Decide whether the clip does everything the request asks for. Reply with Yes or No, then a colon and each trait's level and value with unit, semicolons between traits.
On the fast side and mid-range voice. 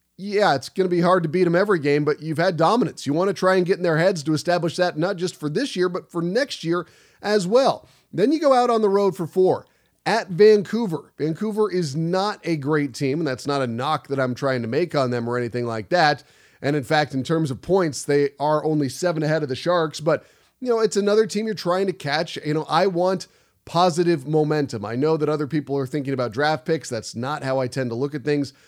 Yes: fast, 255 wpm; medium, 160 Hz